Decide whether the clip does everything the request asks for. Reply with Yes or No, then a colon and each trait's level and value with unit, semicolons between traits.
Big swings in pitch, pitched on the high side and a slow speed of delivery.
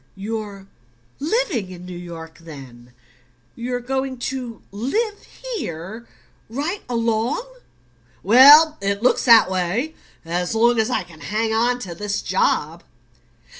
Yes: wide, 6.1 semitones; high, 225 Hz; slow, 125 wpm